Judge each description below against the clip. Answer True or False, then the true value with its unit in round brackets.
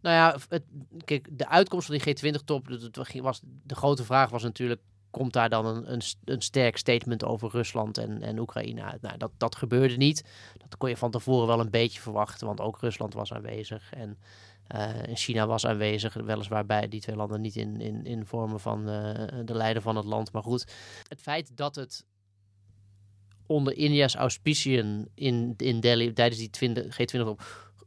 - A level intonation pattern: False (3.4 semitones)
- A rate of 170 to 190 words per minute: True (185 wpm)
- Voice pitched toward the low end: True (115 Hz)